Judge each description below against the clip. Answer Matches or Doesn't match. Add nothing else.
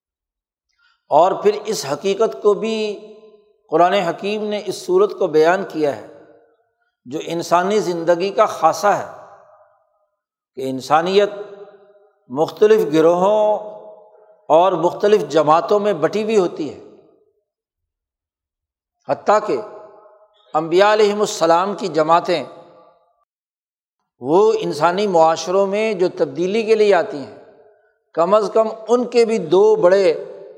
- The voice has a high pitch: Matches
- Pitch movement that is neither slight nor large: Matches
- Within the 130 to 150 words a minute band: Doesn't match